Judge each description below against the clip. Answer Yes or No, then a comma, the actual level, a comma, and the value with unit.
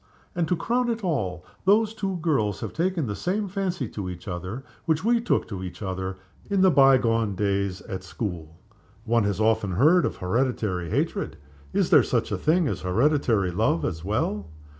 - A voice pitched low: Yes, low, 115 Hz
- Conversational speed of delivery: Yes, average, 185 wpm